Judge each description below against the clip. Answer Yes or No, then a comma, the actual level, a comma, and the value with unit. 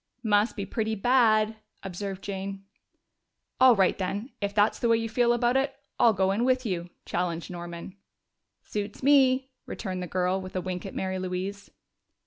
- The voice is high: Yes, high, 200 Hz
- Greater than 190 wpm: No, average, 170 wpm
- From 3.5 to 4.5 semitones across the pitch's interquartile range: Yes, average, 3.8 semitones